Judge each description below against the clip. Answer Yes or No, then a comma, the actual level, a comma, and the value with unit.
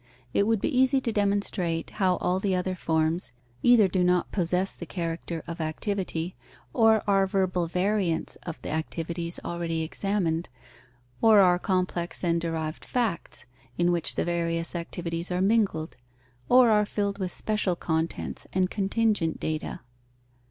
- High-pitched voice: No, medium, 180 Hz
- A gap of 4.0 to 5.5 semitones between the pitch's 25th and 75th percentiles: No, average, 3.3 semitones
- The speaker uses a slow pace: No, average, 145 wpm